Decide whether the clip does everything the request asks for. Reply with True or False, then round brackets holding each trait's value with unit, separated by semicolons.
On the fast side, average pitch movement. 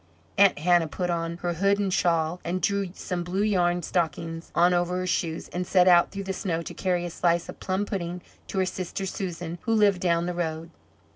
False (215 wpm; 1.8 semitones)